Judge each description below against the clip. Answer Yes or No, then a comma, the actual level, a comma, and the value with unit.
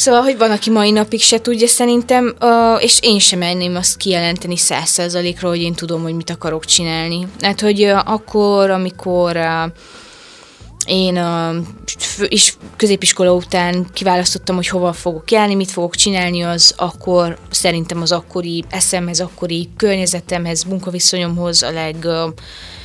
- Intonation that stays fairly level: No, average, 3.3 semitones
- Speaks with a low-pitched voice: No, medium, 180 Hz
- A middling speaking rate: Yes, average, 145 wpm